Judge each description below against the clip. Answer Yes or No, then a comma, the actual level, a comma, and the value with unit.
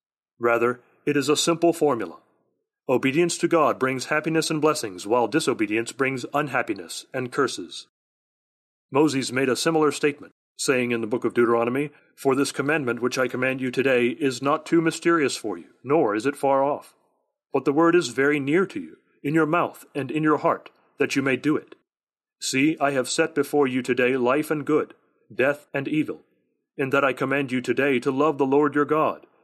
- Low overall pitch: No, medium, 145 Hz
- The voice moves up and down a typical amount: Yes, average, 3.0 semitones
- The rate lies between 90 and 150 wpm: No, average, 190 wpm